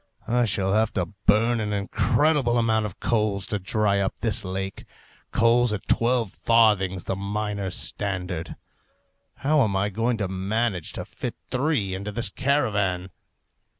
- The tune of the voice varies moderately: Yes, average, 3.1 semitones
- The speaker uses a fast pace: No, average, 150 wpm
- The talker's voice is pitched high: No, low, 105 Hz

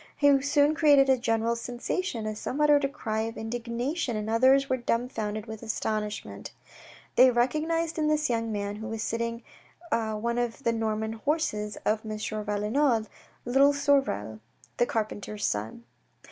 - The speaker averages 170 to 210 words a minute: No, average, 150 wpm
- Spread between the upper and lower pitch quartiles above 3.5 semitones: Yes, average, 4.2 semitones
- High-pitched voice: Yes, high, 230 Hz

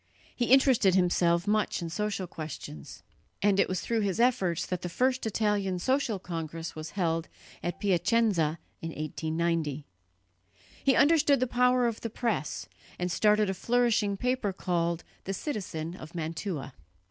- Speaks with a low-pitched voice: No, high, 190 Hz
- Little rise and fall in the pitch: No, wide, 5.5 semitones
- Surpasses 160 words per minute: No, average, 145 wpm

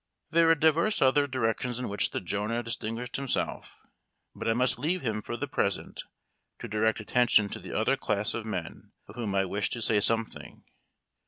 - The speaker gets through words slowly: No, average, 185 wpm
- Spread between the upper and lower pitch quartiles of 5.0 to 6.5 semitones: No, average, 3.5 semitones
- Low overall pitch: Yes, low, 115 Hz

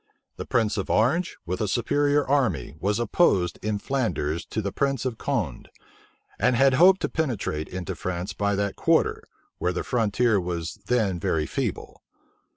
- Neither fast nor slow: Yes, average, 160 wpm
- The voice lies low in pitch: Yes, low, 105 Hz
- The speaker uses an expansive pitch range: Yes, wide, 5.9 semitones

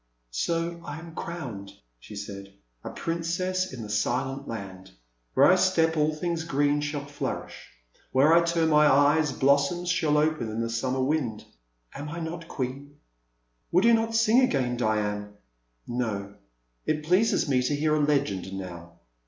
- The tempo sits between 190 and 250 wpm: No, average, 160 wpm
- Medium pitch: Yes, medium, 145 Hz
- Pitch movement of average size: No, wide, 6.3 semitones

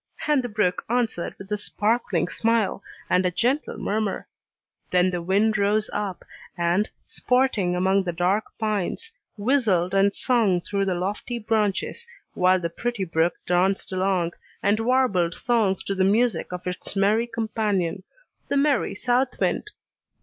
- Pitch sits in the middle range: No, high, 200 Hz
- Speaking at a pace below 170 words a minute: Yes, average, 150 wpm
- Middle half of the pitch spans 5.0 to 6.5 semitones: No, average, 3.9 semitones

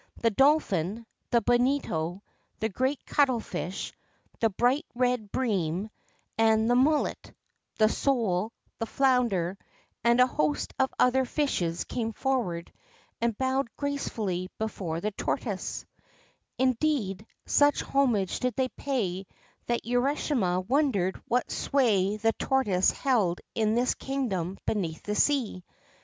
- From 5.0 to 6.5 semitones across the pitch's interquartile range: Yes, average, 5.3 semitones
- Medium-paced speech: No, slow, 120 wpm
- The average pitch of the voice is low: No, high, 230 Hz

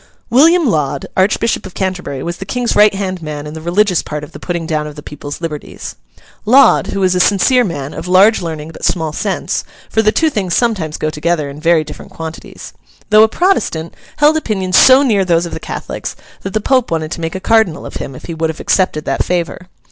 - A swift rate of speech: Yes, fast, 215 wpm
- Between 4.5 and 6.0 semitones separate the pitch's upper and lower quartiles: Yes, average, 5.1 semitones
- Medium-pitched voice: Yes, medium, 180 Hz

